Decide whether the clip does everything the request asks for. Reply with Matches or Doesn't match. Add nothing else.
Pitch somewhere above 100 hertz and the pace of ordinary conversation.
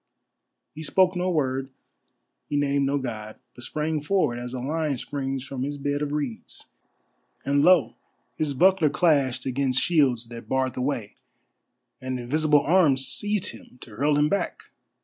Matches